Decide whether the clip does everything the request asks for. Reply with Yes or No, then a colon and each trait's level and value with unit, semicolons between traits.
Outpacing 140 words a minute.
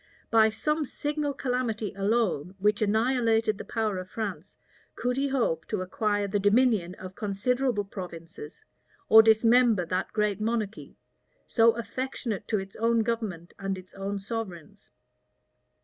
No: slow, 135 wpm